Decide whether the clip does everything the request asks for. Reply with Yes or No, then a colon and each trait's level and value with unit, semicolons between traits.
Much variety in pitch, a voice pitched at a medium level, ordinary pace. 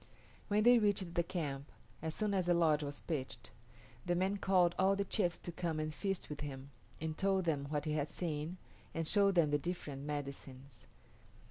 No: average, 4.3 semitones; medium, 165 Hz; average, 195 wpm